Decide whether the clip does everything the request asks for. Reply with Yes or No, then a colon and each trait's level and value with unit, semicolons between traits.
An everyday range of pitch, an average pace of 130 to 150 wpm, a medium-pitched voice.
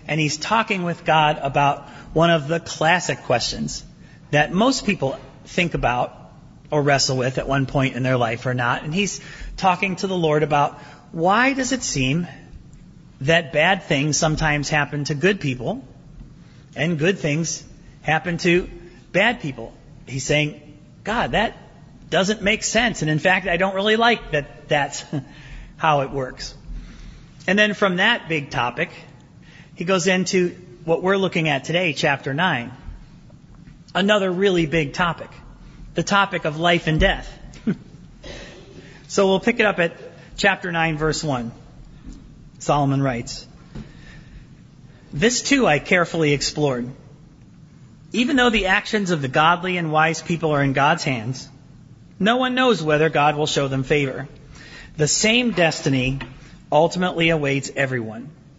Yes: average, 4.0 semitones; average, 145 wpm; medium, 155 Hz